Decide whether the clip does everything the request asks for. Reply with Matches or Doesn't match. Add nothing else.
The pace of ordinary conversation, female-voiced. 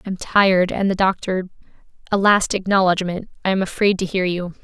Matches